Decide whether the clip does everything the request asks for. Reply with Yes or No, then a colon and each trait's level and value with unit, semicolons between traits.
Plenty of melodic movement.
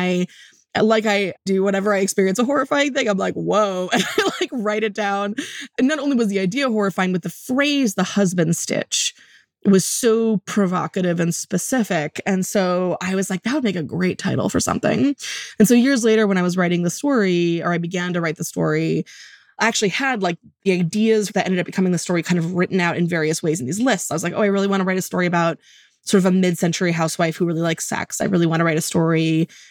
No: average, 3.7 semitones